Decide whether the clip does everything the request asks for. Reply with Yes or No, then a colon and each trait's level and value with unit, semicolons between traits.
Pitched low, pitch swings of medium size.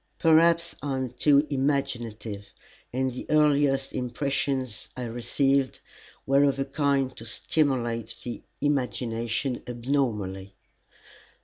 Yes: low, 130 Hz; average, 3.0 semitones